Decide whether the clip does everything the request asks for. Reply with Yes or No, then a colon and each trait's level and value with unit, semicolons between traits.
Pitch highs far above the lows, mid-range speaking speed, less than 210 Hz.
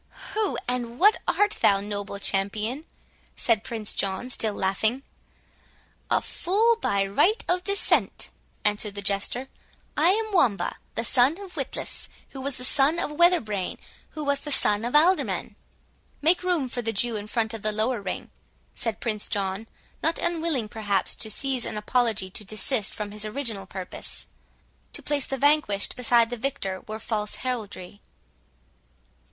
No: wide, 5.8 semitones; average, 160 wpm; high, 230 Hz